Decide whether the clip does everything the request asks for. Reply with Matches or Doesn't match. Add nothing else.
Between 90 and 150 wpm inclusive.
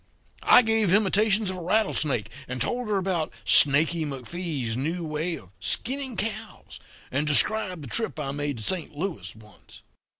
Doesn't match